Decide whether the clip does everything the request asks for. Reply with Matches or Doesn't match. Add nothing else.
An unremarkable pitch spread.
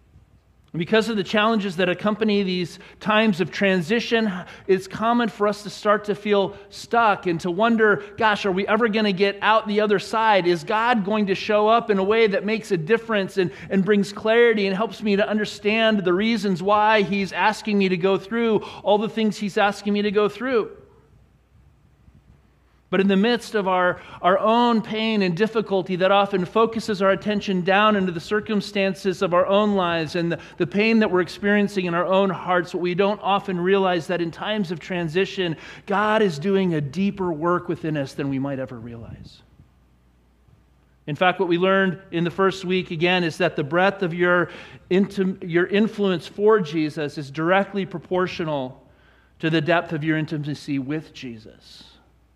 Matches